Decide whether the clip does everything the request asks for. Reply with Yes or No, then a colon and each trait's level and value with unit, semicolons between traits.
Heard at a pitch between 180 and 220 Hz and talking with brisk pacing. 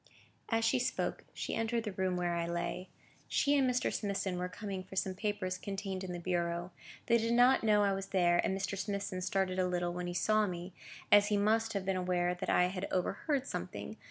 Yes: high, 190 Hz; fast, 215 wpm